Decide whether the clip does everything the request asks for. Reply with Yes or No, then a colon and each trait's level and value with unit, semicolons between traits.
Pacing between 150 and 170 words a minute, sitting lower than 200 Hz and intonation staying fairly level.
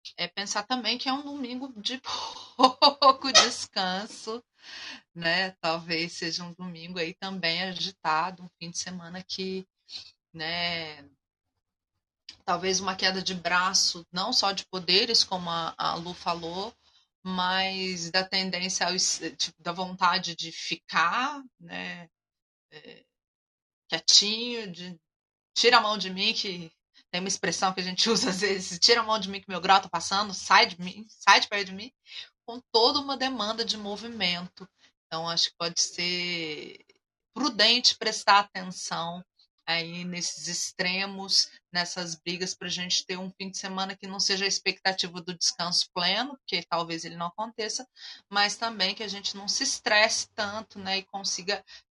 No: average, 155 wpm; high, 190 Hz; average, 3.4 semitones